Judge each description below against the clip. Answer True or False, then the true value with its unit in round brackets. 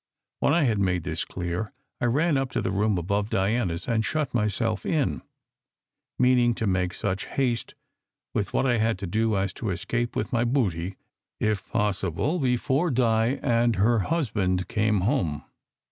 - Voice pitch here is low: True (110 Hz)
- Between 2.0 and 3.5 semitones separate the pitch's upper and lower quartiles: False (4.2 semitones)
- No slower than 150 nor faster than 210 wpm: True (170 wpm)